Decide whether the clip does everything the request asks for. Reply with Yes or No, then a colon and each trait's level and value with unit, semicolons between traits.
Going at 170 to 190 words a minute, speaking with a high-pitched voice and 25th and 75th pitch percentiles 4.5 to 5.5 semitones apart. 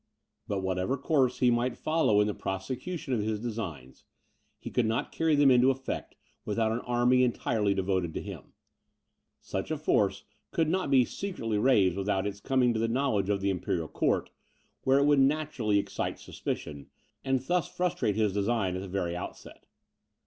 No: average, 175 wpm; low, 115 Hz; average, 5.2 semitones